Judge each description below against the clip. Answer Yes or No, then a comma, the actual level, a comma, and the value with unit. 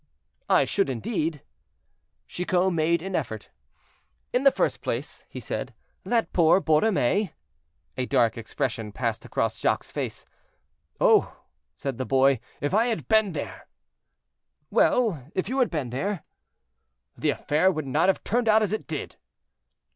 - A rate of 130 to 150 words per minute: Yes, average, 145 wpm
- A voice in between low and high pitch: Yes, medium, 165 Hz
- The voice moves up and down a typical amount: No, wide, 7.4 semitones